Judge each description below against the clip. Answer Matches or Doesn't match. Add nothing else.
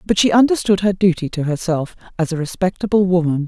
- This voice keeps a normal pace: Matches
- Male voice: Doesn't match